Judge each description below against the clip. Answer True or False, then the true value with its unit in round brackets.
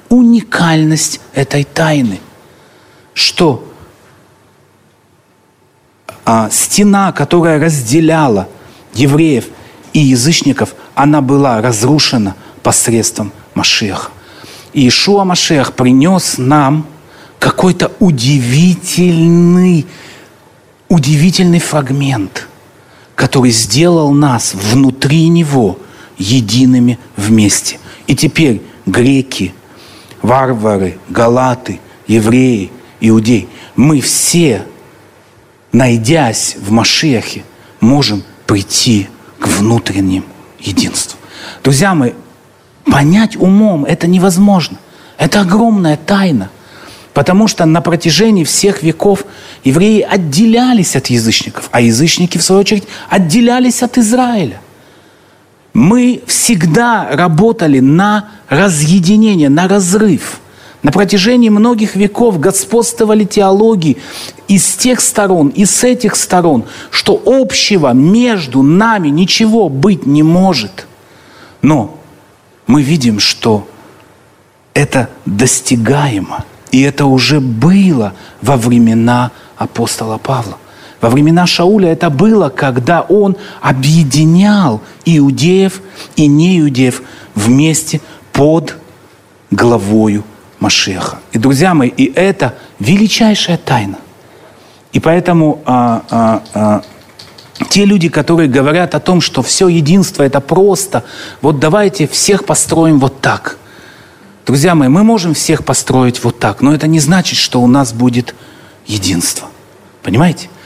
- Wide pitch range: True (7.1 semitones)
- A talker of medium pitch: True (150 Hz)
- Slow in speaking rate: True (100 wpm)